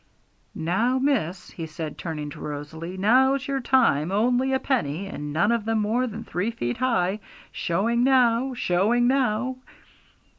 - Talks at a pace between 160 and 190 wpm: No, average, 150 wpm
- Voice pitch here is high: Yes, high, 220 Hz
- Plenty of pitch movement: Yes, wide, 6.7 semitones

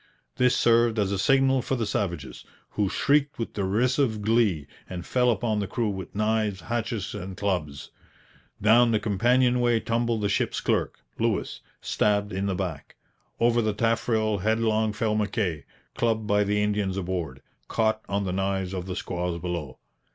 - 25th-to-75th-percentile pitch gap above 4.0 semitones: No, average, 3.2 semitones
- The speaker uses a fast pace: No, average, 160 wpm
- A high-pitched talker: No, low, 105 Hz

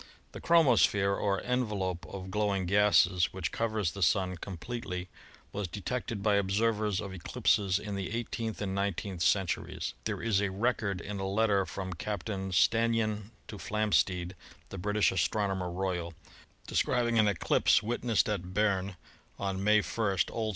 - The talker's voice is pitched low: Yes, low, 100 Hz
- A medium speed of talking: Yes, average, 150 wpm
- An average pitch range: No, narrow, 2.3 semitones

